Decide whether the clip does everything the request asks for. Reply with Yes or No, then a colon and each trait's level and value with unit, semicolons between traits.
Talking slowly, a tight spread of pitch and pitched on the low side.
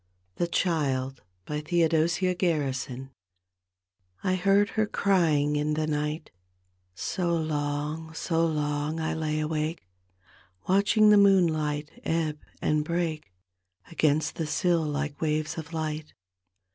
No: slow, 115 wpm; narrow, 2.3 semitones; medium, 155 Hz